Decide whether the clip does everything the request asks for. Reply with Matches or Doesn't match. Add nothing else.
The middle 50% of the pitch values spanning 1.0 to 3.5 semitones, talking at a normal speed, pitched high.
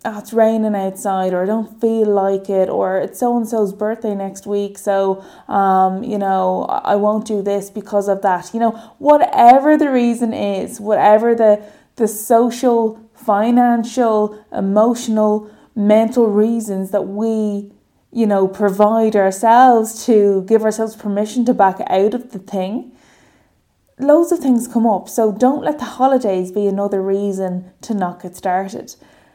Matches